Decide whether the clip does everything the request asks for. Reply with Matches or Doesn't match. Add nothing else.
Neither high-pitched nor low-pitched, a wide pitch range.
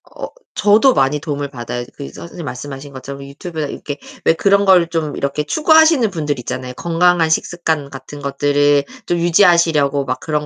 Doesn't match